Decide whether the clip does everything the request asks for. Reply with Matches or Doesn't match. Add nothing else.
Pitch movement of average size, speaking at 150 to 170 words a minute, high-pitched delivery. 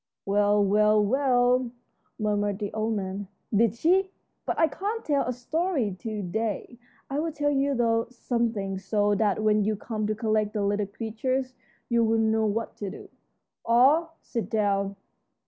Matches